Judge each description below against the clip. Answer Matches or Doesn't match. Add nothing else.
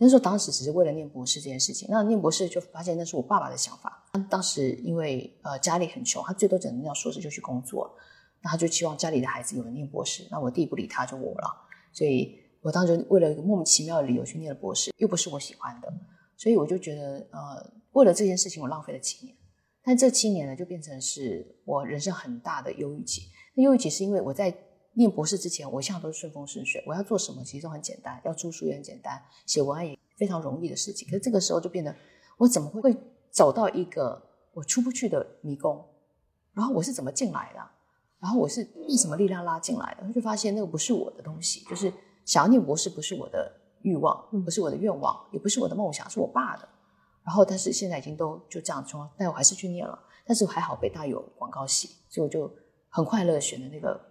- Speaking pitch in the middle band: Matches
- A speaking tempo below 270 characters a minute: Doesn't match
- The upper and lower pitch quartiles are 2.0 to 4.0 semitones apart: Doesn't match